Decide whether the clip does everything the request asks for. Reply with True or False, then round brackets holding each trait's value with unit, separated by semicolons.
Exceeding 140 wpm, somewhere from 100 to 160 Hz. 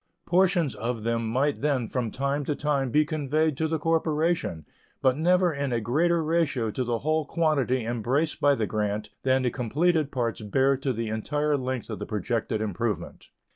True (180 wpm; 135 Hz)